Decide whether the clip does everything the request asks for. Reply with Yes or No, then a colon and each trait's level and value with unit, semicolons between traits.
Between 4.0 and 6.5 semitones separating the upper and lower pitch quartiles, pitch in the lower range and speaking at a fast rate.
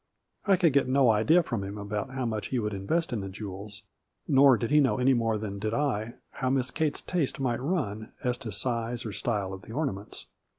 Yes: average, 4.3 semitones; low, 120 Hz; fast, 220 wpm